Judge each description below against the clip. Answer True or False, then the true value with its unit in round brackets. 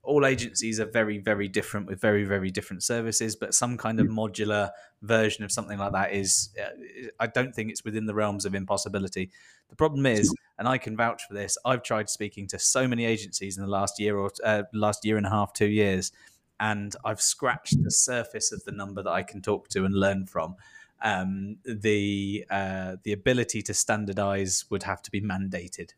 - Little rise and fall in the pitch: True (1.9 semitones)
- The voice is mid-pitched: False (105 Hz)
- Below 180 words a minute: False (205 wpm)